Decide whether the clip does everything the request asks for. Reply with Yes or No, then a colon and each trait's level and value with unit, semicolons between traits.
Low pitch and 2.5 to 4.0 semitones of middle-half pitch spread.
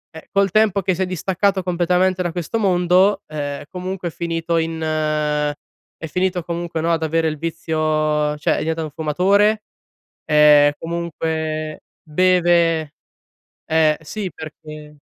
No: medium, 165 Hz; average, 2.8 semitones